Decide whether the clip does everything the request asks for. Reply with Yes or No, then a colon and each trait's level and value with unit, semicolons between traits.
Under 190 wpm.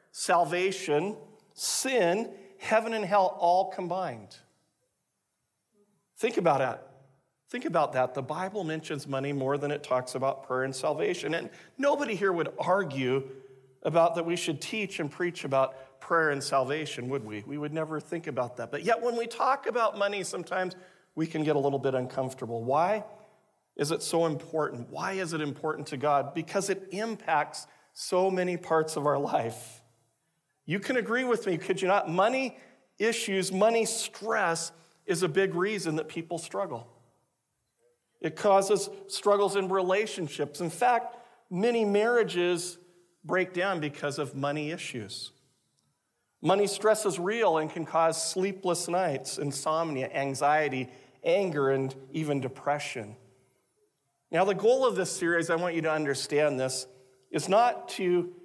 Yes: average, 150 wpm